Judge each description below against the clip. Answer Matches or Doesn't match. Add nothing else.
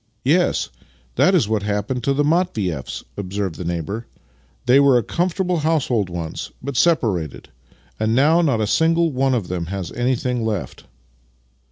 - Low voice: Matches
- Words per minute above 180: Doesn't match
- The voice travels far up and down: Matches